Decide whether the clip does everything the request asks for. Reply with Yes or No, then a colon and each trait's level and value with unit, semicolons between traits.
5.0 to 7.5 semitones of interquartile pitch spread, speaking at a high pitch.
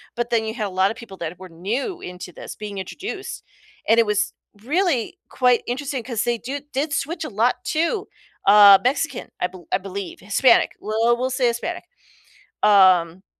Yes: average, 5.3 semitones; high, 230 Hz